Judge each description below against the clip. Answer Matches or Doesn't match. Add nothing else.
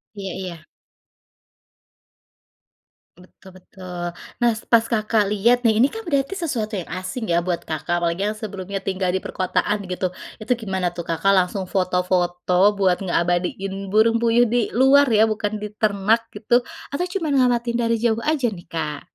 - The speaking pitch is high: Matches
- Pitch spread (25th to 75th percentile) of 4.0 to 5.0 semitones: Matches